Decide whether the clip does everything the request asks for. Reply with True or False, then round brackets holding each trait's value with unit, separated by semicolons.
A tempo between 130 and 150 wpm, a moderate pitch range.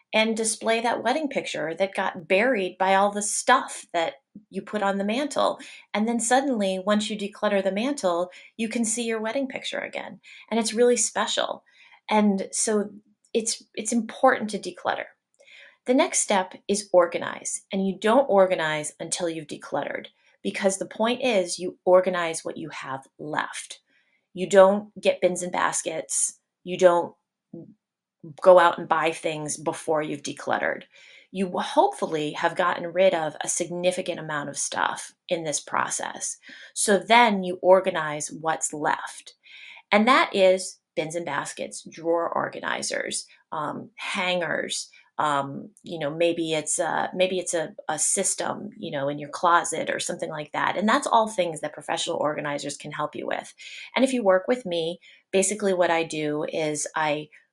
False (165 wpm; 4.0 semitones)